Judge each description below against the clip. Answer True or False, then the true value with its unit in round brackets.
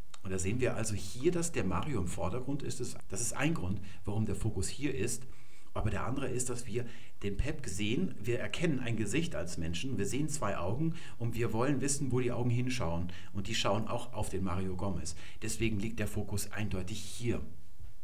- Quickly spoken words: True (205 wpm)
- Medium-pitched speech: False (110 Hz)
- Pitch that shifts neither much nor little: True (4.1 semitones)